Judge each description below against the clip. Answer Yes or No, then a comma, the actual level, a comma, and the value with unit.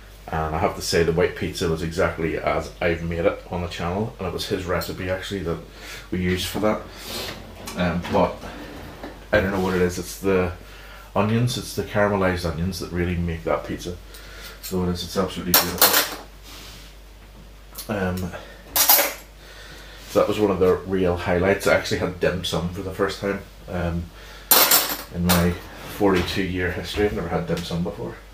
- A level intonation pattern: Yes, narrow, 2.1 semitones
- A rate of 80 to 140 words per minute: No, average, 180 wpm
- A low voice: Yes, very low, 90 Hz